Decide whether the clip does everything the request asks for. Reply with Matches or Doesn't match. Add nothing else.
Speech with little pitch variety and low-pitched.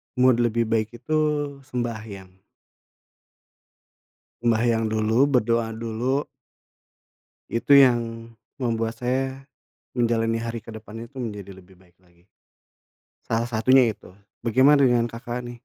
Matches